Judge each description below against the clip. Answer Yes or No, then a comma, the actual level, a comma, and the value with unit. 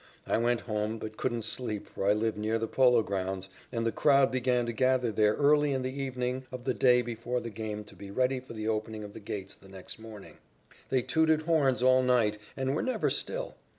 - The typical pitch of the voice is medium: No, low, 120 Hz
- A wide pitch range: No, average, 3.2 semitones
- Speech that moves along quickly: Yes, fast, 220 wpm